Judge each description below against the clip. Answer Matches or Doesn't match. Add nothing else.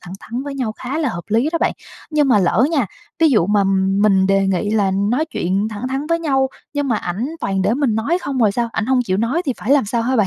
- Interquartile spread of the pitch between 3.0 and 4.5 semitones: Doesn't match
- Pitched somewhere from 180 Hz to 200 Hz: Doesn't match